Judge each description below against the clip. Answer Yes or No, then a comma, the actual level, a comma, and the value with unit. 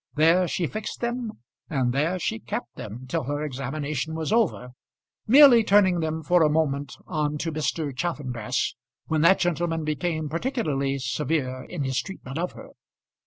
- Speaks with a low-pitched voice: No, medium, 155 Hz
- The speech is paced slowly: No, average, 160 wpm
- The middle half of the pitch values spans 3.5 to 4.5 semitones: Yes, average, 4.2 semitones